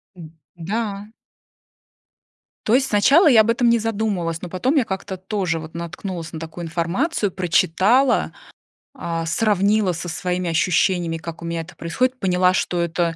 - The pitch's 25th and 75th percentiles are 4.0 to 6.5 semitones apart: Yes, average, 4.5 semitones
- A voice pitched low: No, medium, 185 Hz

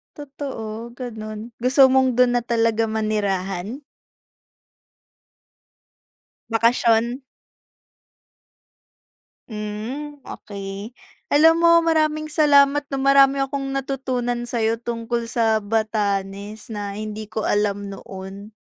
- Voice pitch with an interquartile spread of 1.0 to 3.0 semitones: No, average, 4.2 semitones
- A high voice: Yes, high, 230 Hz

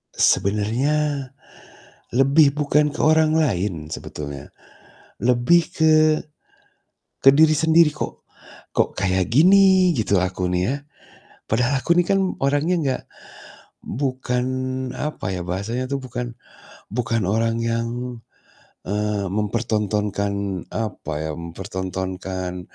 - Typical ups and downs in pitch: No, wide, 6.8 semitones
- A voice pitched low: Yes, low, 115 Hz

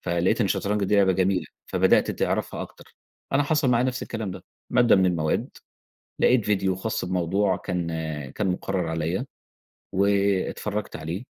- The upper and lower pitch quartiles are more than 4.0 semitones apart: No, average, 2.8 semitones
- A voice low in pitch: Yes, very low, 95 Hz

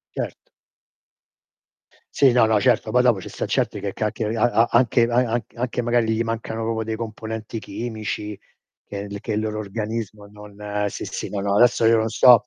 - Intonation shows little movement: Yes, narrow, 2.0 semitones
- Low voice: Yes, low, 110 Hz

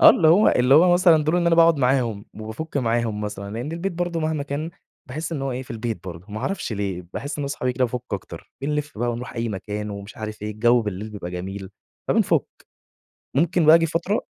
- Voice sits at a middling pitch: No, low, 125 Hz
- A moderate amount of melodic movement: No, wide, 6.9 semitones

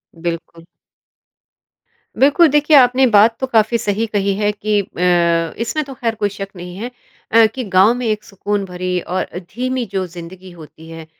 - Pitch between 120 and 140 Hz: No, high, 205 Hz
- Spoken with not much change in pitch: No, average, 4.6 semitones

